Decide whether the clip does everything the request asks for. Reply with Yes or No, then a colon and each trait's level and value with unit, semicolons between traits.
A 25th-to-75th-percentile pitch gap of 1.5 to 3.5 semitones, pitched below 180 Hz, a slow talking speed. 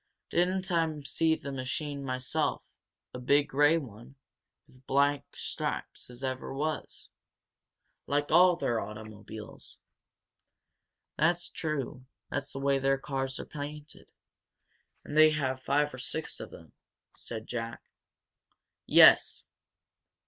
Yes: average, 2.9 semitones; medium, 140 Hz; slow, 120 wpm